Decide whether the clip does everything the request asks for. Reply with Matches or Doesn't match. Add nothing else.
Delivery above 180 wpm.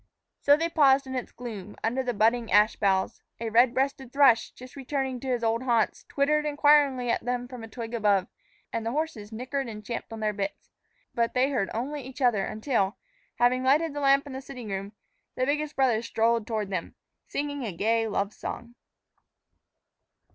Matches